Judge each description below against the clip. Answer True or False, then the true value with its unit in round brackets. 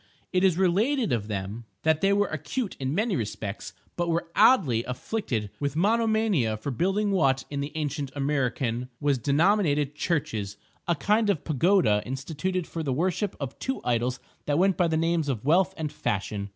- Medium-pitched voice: True (150 Hz)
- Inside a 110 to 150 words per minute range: False (170 wpm)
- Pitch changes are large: True (6.8 semitones)